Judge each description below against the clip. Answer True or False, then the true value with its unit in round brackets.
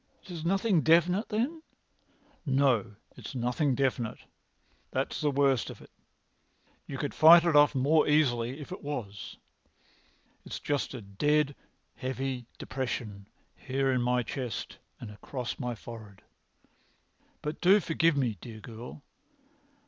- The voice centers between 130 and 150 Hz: True (135 Hz)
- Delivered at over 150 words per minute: False (135 wpm)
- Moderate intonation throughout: True (4.1 semitones)